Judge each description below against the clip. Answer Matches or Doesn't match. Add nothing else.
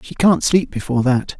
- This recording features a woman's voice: Doesn't match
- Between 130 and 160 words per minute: Doesn't match